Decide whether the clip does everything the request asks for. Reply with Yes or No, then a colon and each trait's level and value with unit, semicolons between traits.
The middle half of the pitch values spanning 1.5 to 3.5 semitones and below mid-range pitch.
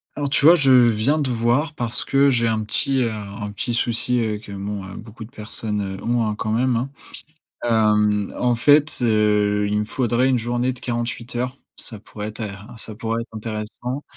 Yes: average, 2.7 semitones; low, 115 Hz